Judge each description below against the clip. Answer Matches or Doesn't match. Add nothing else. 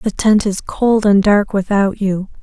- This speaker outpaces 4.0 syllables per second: Doesn't match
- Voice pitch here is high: Matches